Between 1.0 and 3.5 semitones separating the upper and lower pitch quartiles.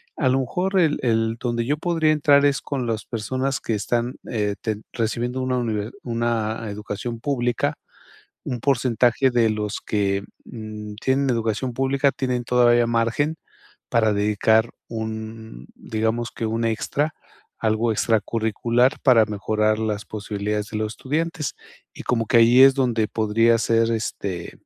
Yes: average, 2.8 semitones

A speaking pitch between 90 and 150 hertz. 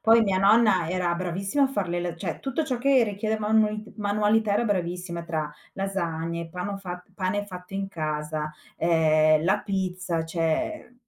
No: medium, 185 Hz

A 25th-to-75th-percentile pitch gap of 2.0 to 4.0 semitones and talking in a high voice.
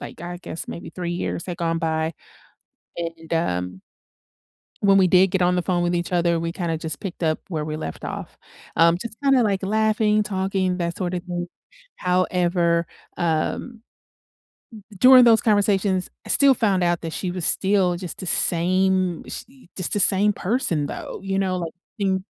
No: narrow, 2.5 semitones; medium, 180 Hz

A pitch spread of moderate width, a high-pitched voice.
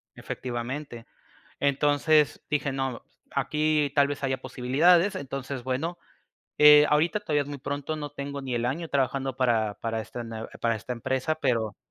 No: average, 3.1 semitones; medium, 140 Hz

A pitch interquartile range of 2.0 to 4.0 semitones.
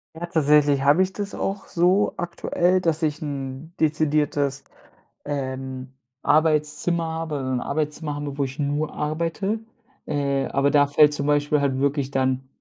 Yes: narrow, 2.5 semitones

